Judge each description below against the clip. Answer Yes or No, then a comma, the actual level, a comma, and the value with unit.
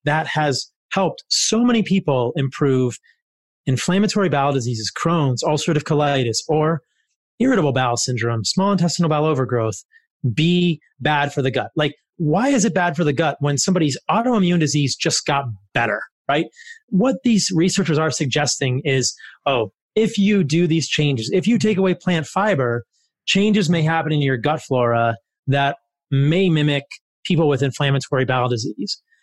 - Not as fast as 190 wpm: Yes, average, 155 wpm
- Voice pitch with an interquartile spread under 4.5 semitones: No, average, 5.2 semitones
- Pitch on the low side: No, medium, 150 Hz